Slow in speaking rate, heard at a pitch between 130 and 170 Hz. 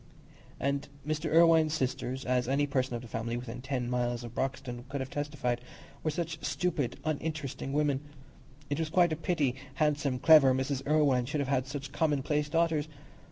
No: average, 165 wpm; medium, 140 Hz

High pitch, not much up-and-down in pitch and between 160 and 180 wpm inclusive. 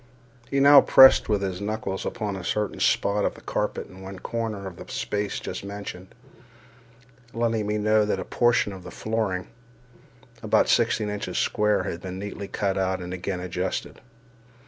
No: low, 100 Hz; narrow, 2.3 semitones; average, 170 wpm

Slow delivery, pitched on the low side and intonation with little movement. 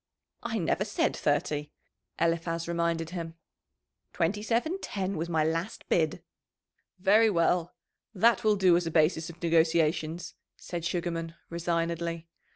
No: slow, 130 wpm; medium, 170 Hz; narrow, 2.1 semitones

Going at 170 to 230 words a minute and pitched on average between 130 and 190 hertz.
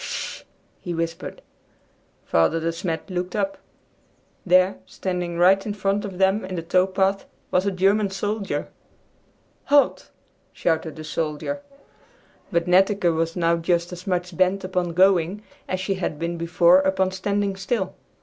No: average, 150 wpm; medium, 185 Hz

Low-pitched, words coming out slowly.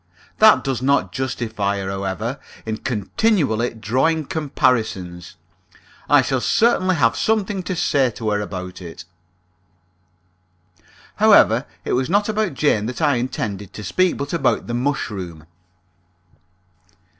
Yes: low, 120 Hz; slow, 125 wpm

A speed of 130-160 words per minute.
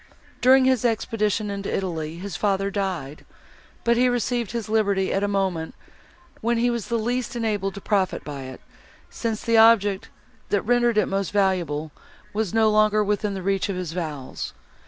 No: average, 175 wpm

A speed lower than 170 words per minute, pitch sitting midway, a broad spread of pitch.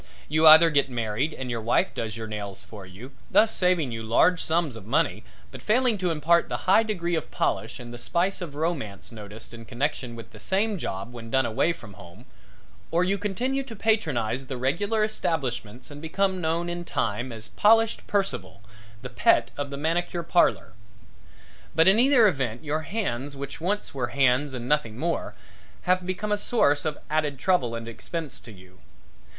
No: average, 185 wpm; medium, 145 Hz; wide, 7.3 semitones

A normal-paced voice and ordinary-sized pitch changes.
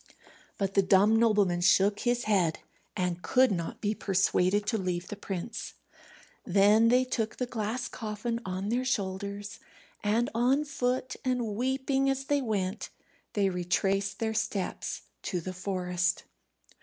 Yes: average, 145 wpm; average, 4.1 semitones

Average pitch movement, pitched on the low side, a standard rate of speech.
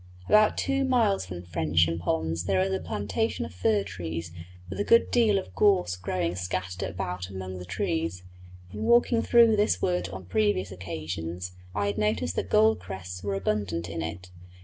Yes: average, 3.3 semitones; very low, 95 Hz; average, 175 wpm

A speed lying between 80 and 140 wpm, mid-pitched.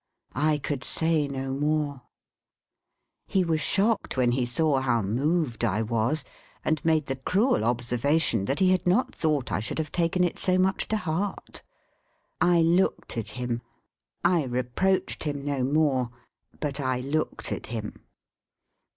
No: average, 150 wpm; medium, 145 Hz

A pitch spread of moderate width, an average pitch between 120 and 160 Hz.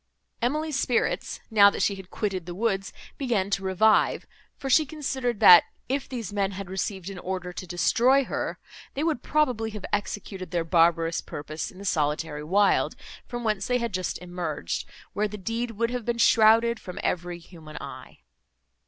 No: average, 4.7 semitones; high, 200 Hz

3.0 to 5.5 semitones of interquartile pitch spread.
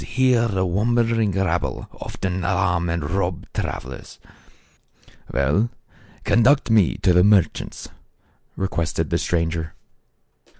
Yes: average, 4.7 semitones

